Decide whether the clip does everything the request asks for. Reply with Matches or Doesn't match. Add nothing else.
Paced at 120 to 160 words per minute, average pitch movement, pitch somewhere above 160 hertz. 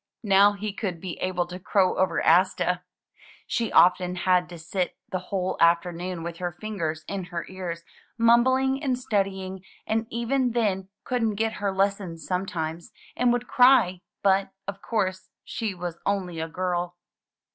Matches